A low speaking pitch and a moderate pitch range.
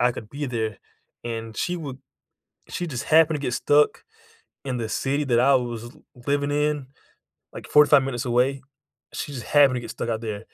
Yes: low, 130 Hz; average, 3.5 semitones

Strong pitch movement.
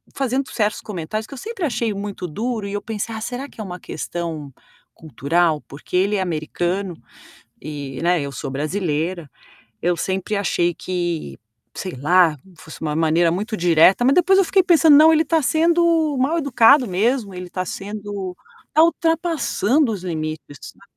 Yes: wide, 7.5 semitones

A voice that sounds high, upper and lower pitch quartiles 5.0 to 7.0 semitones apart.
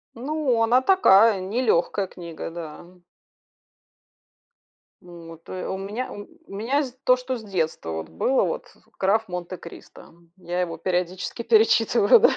Yes: high, 195 Hz; wide, 5.4 semitones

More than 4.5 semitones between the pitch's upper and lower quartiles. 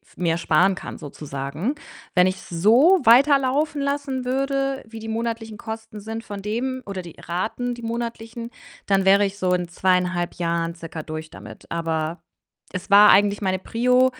Yes: average, 5.2 semitones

